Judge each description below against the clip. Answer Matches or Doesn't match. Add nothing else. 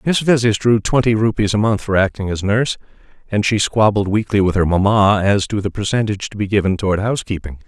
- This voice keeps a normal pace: Doesn't match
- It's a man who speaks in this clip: Matches